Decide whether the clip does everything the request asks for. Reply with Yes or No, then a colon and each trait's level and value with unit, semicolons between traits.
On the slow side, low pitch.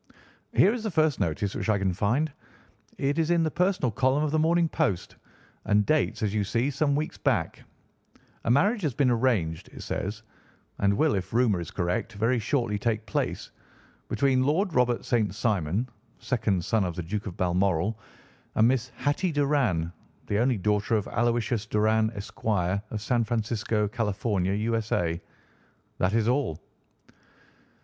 No: average, 160 wpm; low, 115 Hz